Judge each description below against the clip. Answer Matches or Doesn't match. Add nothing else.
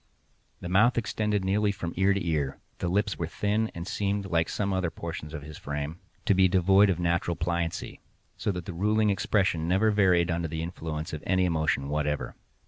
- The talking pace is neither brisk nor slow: Matches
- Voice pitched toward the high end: Doesn't match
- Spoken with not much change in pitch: Doesn't match